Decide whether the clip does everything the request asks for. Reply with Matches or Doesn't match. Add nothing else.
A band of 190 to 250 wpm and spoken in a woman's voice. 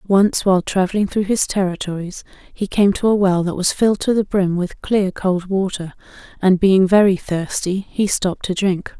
Matches